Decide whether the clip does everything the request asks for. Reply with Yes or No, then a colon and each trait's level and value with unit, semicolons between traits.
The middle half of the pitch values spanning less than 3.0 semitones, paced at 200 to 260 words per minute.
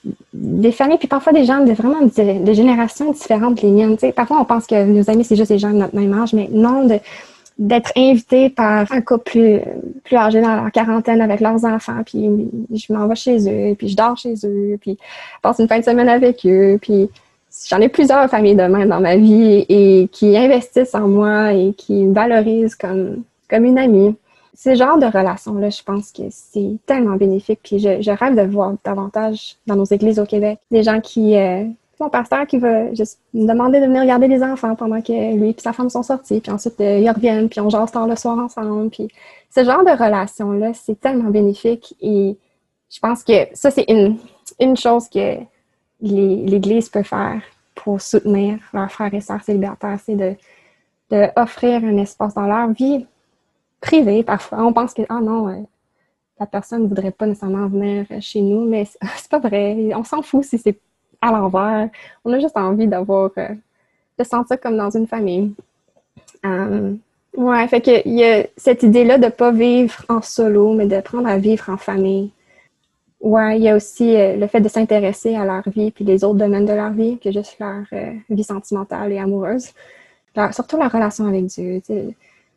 Yes: narrow, 2.6 semitones; average, 205 wpm